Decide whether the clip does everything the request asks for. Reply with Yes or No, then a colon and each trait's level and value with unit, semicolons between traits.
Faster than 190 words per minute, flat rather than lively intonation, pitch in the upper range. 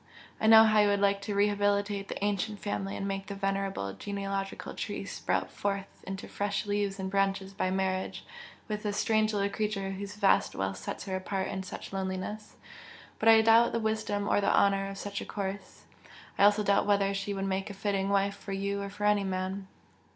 Yes: average, 200 wpm; narrow, 1.0 semitones; high, 200 Hz